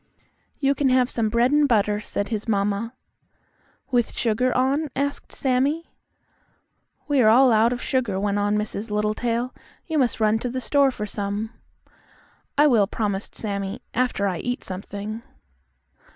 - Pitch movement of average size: Yes, average, 3.7 semitones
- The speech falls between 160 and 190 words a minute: No, average, 150 wpm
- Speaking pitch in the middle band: No, high, 230 Hz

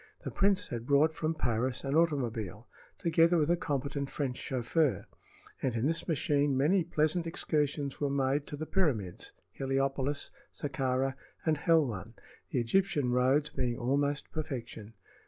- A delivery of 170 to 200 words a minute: No, average, 140 wpm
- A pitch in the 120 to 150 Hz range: Yes, medium, 140 Hz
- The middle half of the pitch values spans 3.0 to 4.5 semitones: Yes, average, 3.6 semitones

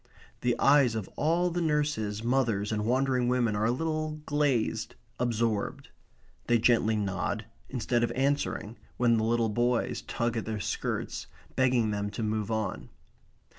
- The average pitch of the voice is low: Yes, low, 120 Hz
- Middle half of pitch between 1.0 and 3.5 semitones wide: Yes, average, 3.2 semitones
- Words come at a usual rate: Yes, average, 150 wpm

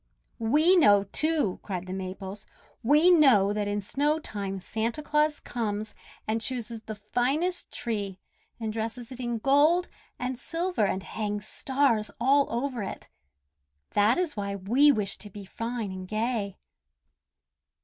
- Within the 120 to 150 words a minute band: Yes, average, 145 wpm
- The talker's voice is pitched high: Yes, high, 225 Hz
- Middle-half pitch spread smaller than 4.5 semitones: No, wide, 5.5 semitones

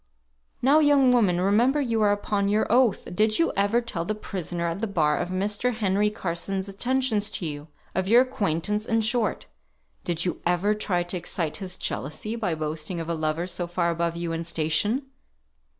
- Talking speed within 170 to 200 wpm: Yes, average, 185 wpm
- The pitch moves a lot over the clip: No, average, 4.3 semitones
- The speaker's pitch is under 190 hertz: No, high, 195 Hz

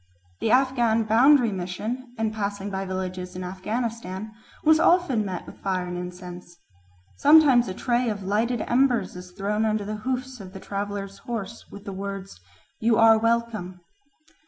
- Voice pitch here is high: Yes, high, 210 Hz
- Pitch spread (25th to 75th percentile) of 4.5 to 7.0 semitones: No, average, 3.9 semitones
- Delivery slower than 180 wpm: Yes, average, 160 wpm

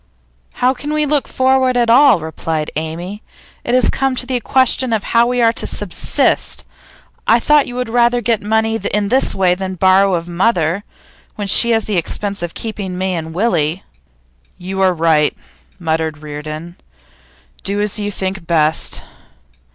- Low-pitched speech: No, high, 200 Hz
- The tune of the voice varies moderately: No, wide, 5.7 semitones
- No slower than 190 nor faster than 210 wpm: No, average, 165 wpm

